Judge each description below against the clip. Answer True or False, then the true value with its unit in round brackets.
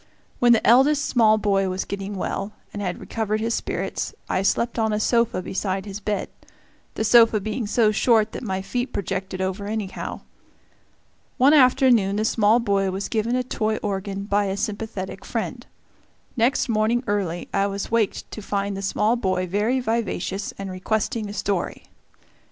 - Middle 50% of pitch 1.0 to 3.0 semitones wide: True (2.7 semitones)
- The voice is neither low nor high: False (210 Hz)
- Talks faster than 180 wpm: False (170 wpm)